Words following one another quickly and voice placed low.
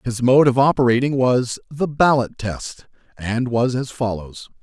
No: average, 155 wpm; low, 125 Hz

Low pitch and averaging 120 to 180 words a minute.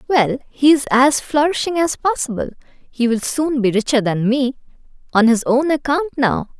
No: very high, 265 Hz; average, 165 wpm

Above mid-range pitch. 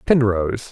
No: low, 115 Hz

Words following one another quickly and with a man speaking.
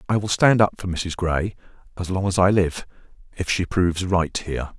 Yes: fast, 215 wpm; male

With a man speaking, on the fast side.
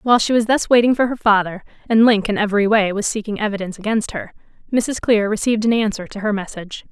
No: female; fast, 225 wpm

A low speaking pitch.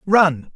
No: medium, 175 Hz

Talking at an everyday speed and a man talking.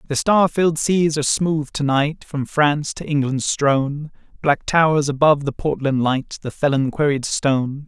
Yes: average, 175 wpm; male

